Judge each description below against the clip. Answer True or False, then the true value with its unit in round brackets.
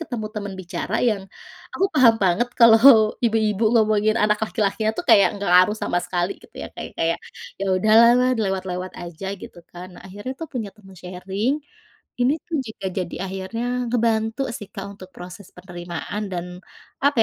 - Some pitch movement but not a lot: True (3.4 semitones)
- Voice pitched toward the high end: True (205 Hz)